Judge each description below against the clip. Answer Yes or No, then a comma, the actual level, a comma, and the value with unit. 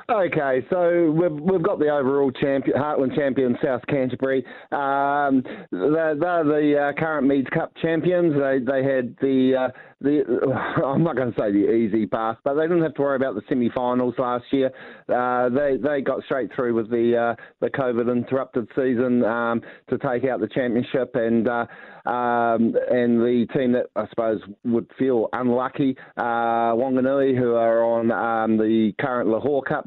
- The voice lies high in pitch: No, low, 130 Hz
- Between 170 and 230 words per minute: Yes, average, 175 wpm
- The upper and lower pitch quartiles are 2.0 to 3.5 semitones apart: Yes, average, 3.1 semitones